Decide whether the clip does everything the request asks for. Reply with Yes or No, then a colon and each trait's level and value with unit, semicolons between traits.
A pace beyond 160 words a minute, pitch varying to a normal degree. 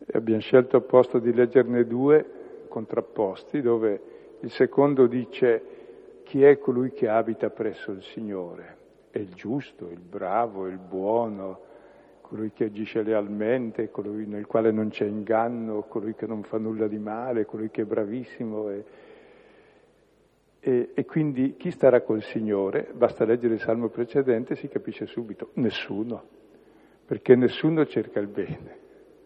No: average, 145 wpm; average, 4.3 semitones